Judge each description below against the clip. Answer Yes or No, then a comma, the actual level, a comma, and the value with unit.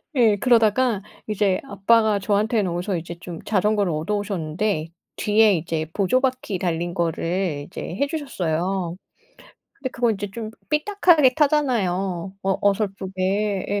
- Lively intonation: No, average, 4.0 semitones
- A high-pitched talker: Yes, high, 200 Hz